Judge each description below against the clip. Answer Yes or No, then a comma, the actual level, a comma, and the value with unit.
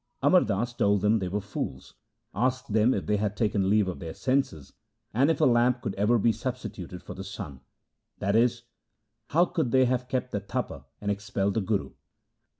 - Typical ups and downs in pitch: Yes, average, 3.9 semitones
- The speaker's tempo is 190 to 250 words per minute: Yes, average, 195 wpm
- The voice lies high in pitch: No, low, 105 Hz